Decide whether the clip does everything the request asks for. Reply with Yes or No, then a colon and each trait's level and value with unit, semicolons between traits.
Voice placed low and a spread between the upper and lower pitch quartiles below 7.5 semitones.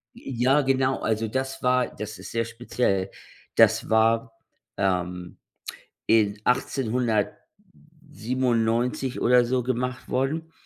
Yes: low, 125 Hz; average, 2.9 semitones